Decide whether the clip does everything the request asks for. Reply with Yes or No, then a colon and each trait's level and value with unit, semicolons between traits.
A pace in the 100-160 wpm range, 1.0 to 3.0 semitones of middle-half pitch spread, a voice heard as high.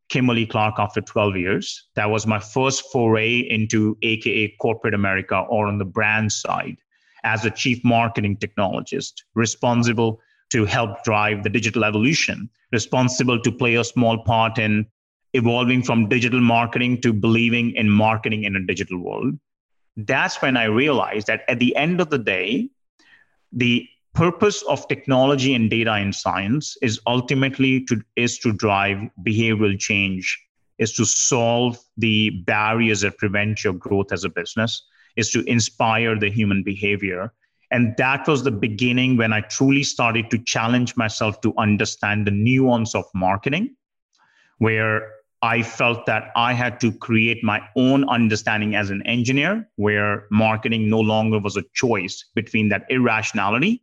No: average, 155 wpm; narrow, 2.5 semitones; low, 115 Hz